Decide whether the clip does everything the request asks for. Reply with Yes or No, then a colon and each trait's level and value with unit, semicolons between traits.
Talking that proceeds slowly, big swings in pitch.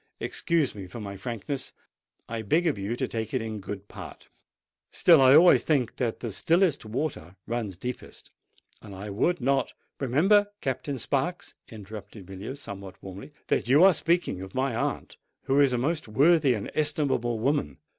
No: average, 165 wpm; wide, 6.0 semitones